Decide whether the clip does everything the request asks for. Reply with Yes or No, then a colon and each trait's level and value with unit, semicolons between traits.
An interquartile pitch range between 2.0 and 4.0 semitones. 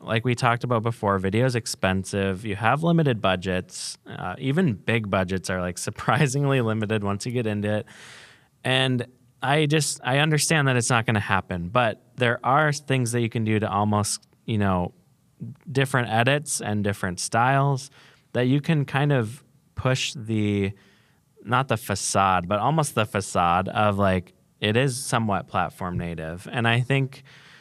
No: average, 4.8 semitones